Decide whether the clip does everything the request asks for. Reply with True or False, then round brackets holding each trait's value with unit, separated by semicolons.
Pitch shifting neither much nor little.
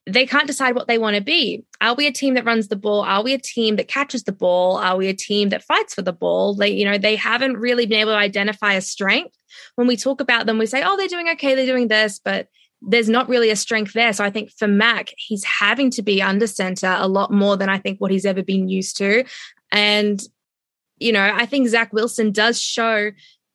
True (3.2 semitones)